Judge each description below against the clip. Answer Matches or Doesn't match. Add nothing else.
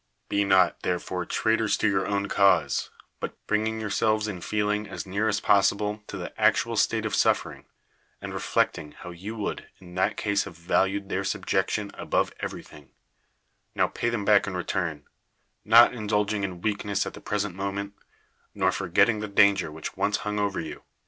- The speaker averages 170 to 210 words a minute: Matches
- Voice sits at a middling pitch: Doesn't match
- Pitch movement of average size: Doesn't match